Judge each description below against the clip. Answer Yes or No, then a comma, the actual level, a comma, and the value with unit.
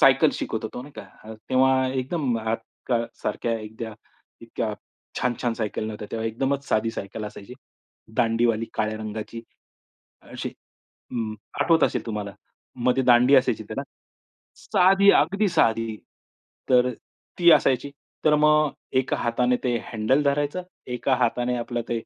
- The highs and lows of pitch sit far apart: No, average, 3.1 semitones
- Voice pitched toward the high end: No, low, 120 Hz